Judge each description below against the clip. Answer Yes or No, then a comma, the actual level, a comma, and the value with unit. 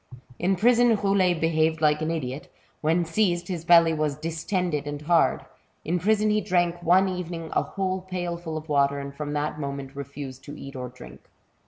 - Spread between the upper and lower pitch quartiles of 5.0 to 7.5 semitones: No, average, 3.6 semitones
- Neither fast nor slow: Yes, average, 180 wpm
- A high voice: No, medium, 165 Hz